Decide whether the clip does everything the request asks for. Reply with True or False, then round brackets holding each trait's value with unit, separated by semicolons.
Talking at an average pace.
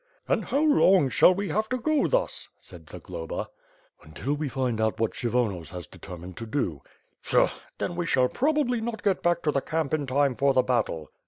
True (195 wpm)